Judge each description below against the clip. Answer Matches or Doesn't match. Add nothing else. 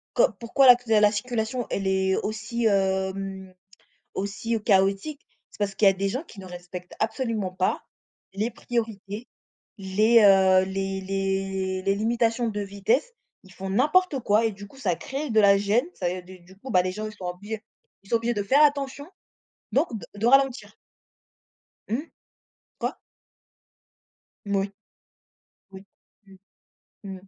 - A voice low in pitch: Doesn't match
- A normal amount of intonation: Matches